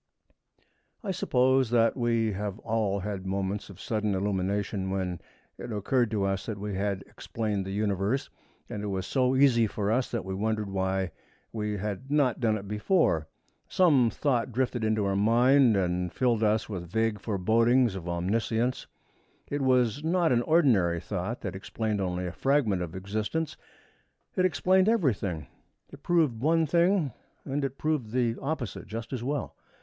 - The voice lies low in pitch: Yes, low, 110 Hz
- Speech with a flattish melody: No, average, 4.9 semitones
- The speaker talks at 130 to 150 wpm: No, average, 165 wpm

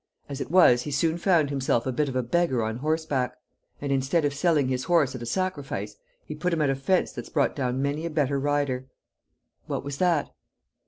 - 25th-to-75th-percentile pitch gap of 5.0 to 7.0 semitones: No, average, 3.6 semitones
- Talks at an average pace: No, fast, 215 wpm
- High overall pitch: No, medium, 140 Hz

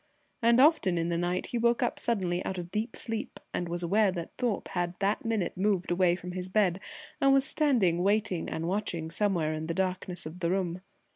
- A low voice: No, medium, 185 Hz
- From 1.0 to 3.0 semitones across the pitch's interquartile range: No, average, 3.8 semitones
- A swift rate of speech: Yes, fast, 210 wpm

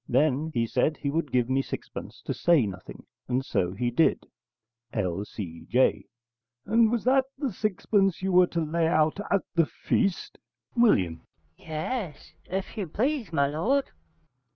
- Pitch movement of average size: No, wide, 7.7 semitones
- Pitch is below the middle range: No, medium, 160 Hz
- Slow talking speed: No, average, 150 wpm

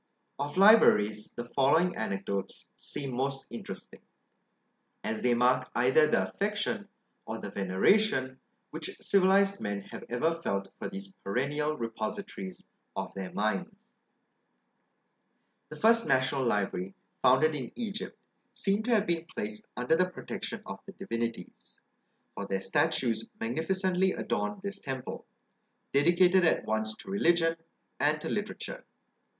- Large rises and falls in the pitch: Yes, wide, 8.6 semitones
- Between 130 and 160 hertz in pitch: Yes, medium, 140 Hz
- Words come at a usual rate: No, slow, 130 wpm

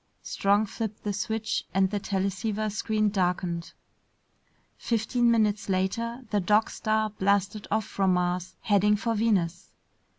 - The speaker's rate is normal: No, slow, 130 wpm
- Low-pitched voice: No, high, 205 Hz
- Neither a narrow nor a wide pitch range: No, narrow, 2.2 semitones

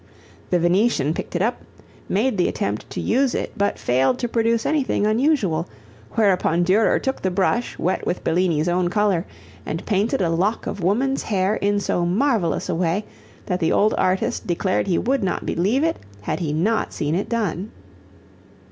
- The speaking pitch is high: Yes, high, 195 Hz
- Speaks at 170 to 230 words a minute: Yes, average, 175 wpm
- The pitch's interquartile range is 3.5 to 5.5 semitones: Yes, average, 4.5 semitones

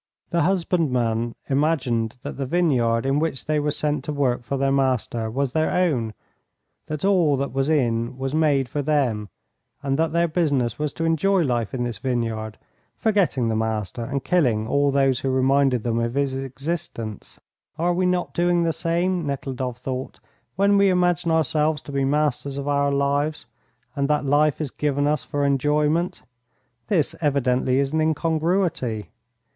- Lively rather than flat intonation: No, average, 3.9 semitones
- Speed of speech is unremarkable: Yes, average, 170 wpm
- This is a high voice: No, medium, 140 Hz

